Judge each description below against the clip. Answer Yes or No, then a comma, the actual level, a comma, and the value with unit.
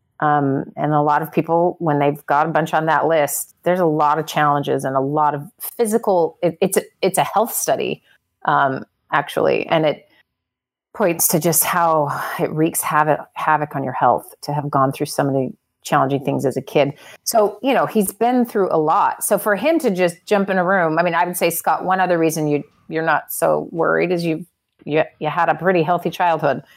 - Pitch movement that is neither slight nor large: Yes, average, 3.4 semitones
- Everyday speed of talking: No, fast, 215 wpm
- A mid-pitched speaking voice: Yes, medium, 160 Hz